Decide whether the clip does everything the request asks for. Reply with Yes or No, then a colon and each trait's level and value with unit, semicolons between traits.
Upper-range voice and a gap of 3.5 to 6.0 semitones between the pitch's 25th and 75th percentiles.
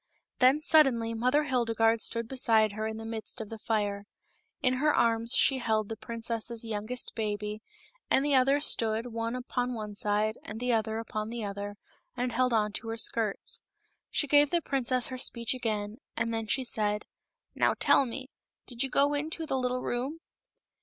No: high, 230 Hz; average, 2.8 semitones